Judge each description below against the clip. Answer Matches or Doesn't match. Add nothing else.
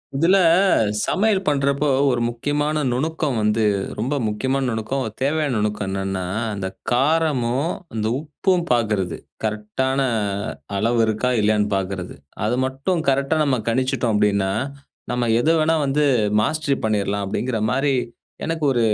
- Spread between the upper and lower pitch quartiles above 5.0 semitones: Matches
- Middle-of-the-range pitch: Doesn't match